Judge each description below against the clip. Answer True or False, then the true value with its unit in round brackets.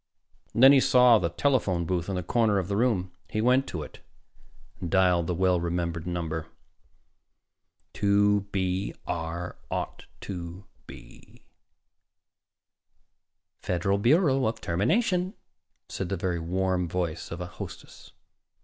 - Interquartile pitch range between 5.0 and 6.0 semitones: False (3.8 semitones)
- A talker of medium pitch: False (95 Hz)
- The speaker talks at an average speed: False (130 wpm)